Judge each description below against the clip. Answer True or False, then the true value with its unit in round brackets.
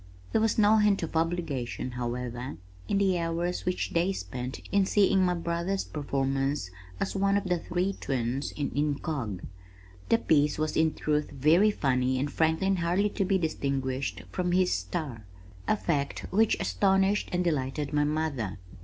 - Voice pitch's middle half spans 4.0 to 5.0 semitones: False (5.6 semitones)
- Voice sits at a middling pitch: True (160 Hz)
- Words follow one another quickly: False (160 wpm)